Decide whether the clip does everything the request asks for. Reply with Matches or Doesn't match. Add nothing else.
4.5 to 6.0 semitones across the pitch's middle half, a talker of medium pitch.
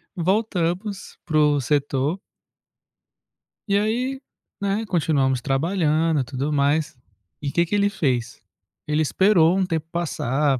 Matches